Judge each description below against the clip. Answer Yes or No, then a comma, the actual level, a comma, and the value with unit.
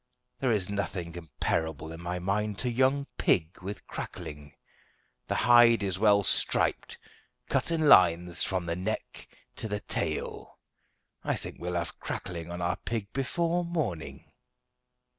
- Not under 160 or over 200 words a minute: No, average, 140 wpm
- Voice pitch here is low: Yes, very low, 95 Hz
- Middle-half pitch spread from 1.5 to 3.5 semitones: No, average, 5.2 semitones